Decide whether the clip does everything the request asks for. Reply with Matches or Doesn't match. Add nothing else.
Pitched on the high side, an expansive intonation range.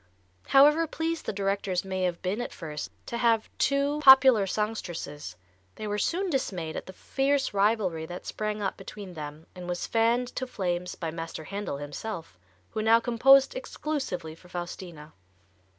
Matches